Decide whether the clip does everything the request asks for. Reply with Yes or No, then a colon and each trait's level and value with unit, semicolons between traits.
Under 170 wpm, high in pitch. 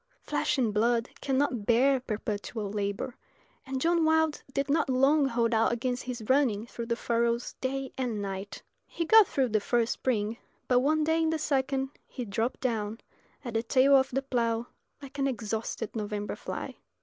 No: average, 175 wpm; high, 245 Hz